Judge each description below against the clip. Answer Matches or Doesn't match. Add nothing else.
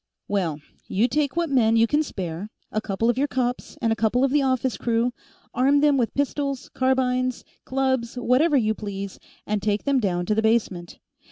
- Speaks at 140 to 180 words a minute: Doesn't match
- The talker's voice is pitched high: Matches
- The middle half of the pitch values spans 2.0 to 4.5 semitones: Matches